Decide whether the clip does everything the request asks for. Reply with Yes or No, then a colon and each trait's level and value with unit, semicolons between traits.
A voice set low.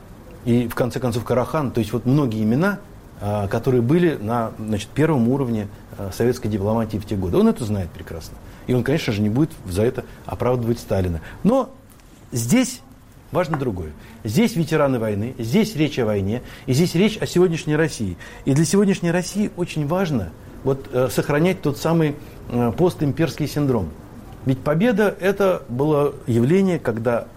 Yes: low, 125 Hz